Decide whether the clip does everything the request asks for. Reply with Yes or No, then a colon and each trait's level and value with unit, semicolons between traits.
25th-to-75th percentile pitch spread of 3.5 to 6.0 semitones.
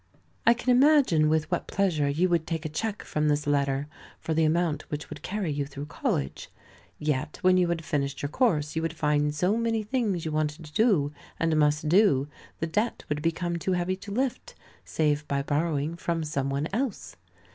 Yes: average, 3.8 semitones